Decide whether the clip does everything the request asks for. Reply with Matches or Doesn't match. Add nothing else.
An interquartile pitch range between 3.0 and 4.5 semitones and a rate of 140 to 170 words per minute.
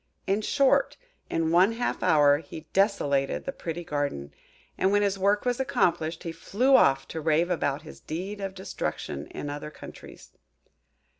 Doesn't match